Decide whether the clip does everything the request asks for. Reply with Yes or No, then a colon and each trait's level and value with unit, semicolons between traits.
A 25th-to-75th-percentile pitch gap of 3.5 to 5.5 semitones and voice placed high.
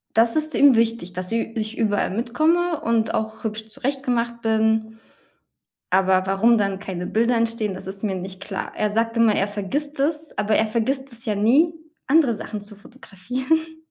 Yes: average, 3.9 semitones; high, 225 Hz